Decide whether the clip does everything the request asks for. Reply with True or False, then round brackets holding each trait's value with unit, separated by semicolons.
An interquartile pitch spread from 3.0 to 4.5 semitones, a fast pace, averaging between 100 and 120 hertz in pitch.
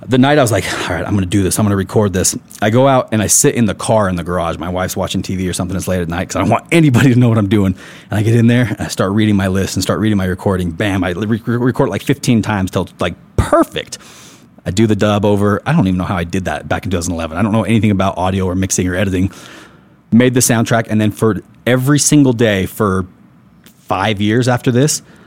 True (3.8 semitones; 275 wpm; 105 Hz)